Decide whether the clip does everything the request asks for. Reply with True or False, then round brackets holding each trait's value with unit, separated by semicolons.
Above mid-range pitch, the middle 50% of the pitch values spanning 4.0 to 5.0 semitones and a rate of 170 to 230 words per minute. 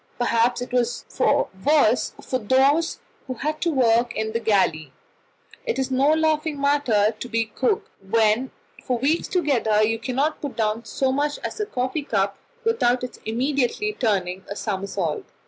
False (250 Hz; 4.7 semitones; 160 wpm)